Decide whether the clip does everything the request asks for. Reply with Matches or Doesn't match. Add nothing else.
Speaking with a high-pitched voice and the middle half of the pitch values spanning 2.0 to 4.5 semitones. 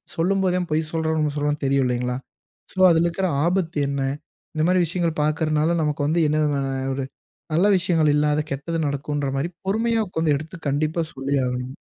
Doesn't match